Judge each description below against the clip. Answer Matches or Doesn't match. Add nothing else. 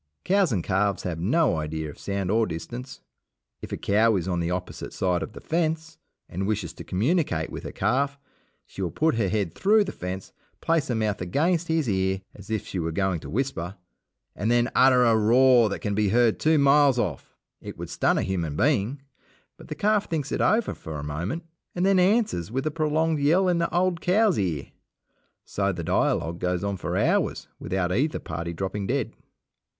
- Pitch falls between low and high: Doesn't match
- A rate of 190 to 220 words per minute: Matches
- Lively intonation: Matches